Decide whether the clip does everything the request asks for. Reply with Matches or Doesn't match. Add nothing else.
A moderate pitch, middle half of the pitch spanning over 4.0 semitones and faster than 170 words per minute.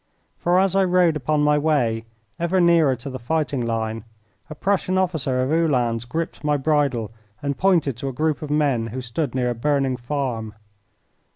Matches